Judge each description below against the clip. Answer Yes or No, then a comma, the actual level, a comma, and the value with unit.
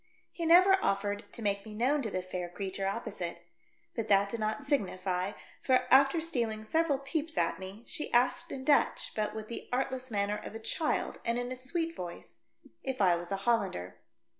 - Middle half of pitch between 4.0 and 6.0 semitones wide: Yes, wide, 5.4 semitones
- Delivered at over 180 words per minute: Yes, average, 190 wpm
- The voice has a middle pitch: No, high, 220 Hz